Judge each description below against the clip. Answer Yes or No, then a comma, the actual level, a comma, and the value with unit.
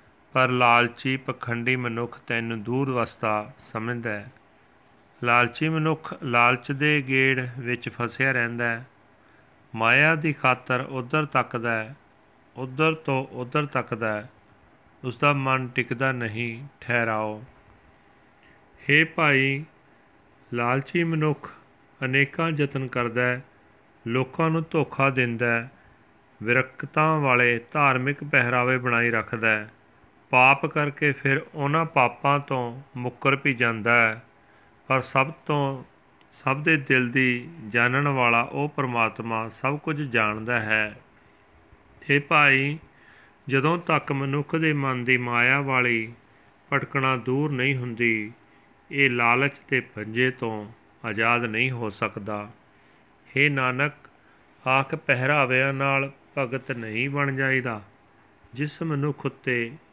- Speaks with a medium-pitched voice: No, low, 130 Hz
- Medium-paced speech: Yes, average, 115 wpm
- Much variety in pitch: No, average, 2.9 semitones